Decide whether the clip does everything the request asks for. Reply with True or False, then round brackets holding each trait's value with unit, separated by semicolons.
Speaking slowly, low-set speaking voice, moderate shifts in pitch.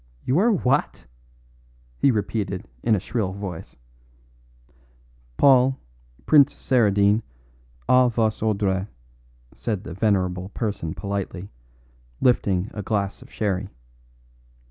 True (100 wpm; 105 Hz; 3.9 semitones)